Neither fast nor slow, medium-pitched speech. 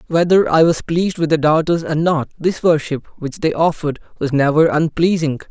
Yes: average, 185 wpm; medium, 160 Hz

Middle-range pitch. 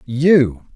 No: low, 125 Hz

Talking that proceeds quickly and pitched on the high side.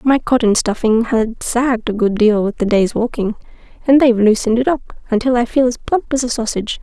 Yes: fast, 220 wpm; high, 235 Hz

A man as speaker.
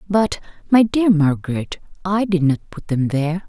No: female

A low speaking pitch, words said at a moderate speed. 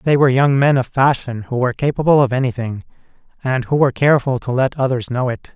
No: low, 130 Hz; fast, 215 wpm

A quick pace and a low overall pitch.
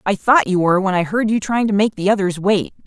No: fast, 295 wpm; high, 200 Hz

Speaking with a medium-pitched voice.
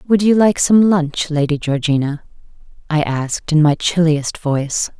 Yes: medium, 160 Hz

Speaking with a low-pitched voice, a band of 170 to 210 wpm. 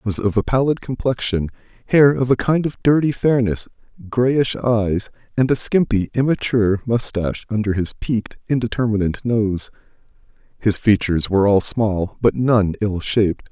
No: low, 115 Hz; average, 150 wpm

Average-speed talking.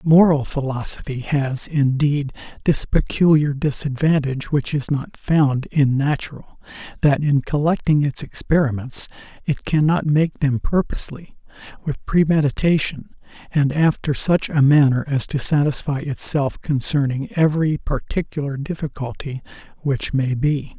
No: slow, 120 wpm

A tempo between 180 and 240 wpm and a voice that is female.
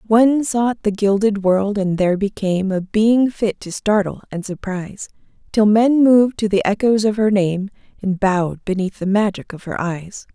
Yes: average, 185 wpm; female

